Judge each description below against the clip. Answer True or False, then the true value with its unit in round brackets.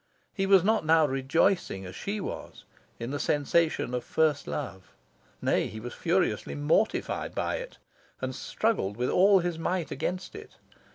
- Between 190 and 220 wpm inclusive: False (160 wpm)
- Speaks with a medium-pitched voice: True (165 Hz)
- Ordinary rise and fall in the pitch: False (6.4 semitones)